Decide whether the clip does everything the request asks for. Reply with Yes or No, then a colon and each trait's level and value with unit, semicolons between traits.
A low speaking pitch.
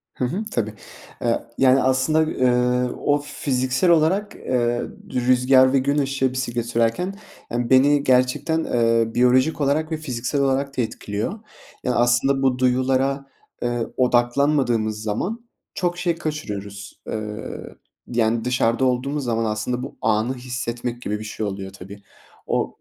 Yes: low, 125 Hz